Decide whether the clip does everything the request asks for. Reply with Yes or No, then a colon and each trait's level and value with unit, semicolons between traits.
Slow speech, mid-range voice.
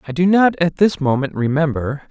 No: average, 200 wpm; medium, 155 Hz